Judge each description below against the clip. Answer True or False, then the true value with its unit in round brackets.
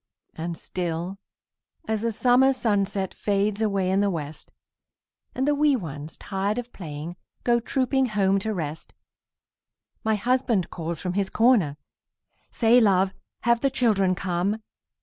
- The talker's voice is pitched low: False (200 Hz)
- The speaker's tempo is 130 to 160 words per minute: True (140 wpm)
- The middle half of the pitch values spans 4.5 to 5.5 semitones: True (4.8 semitones)